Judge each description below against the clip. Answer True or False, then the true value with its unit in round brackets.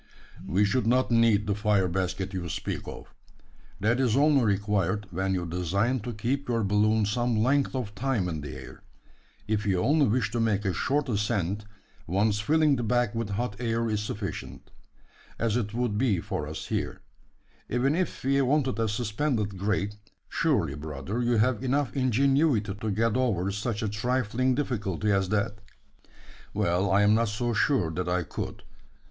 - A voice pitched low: True (110 Hz)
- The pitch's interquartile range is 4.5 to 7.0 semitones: False (3.8 semitones)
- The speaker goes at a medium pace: True (170 wpm)